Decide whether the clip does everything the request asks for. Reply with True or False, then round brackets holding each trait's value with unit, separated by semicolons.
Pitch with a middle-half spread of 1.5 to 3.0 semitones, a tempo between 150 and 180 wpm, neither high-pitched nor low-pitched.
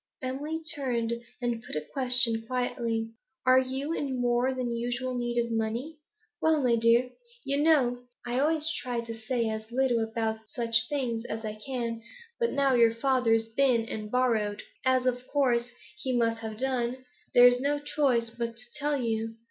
False (2.4 semitones; 170 wpm; 245 Hz)